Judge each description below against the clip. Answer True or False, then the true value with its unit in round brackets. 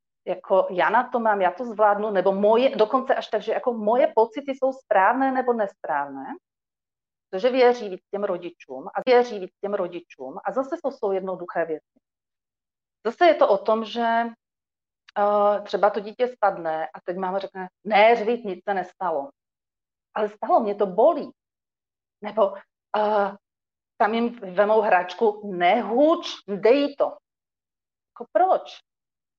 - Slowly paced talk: False (150 wpm)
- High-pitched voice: True (210 Hz)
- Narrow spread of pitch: False (4.3 semitones)